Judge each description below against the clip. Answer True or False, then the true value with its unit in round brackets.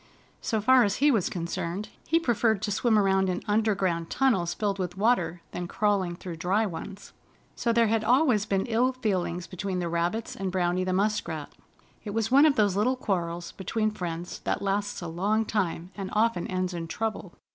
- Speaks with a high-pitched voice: True (195 Hz)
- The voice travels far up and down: False (3.7 semitones)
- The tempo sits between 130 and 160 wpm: False (190 wpm)